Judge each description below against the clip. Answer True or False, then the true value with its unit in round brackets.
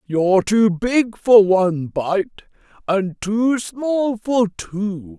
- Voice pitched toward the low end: False (215 Hz)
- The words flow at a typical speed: False (125 wpm)